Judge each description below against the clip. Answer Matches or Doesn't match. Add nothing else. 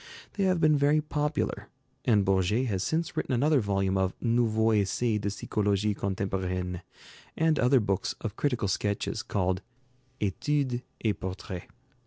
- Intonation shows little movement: Doesn't match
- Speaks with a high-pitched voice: Doesn't match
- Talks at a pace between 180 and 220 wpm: Doesn't match